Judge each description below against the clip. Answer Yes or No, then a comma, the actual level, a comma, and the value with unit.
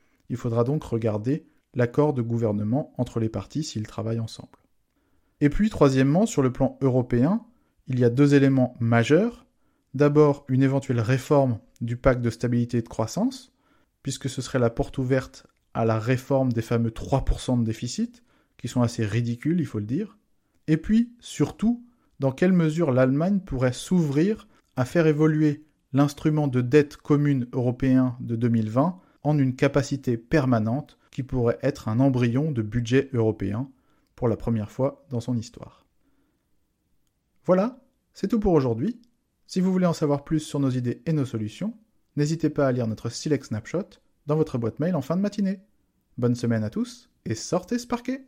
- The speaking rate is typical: Yes, average, 170 wpm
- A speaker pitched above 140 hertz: No, low, 135 Hz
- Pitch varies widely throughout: No, average, 4.7 semitones